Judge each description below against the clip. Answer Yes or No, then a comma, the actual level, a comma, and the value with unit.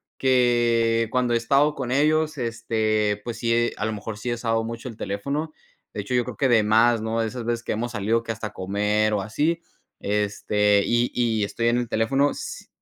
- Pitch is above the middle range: No, low, 115 Hz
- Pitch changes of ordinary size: No, narrow, 2.3 semitones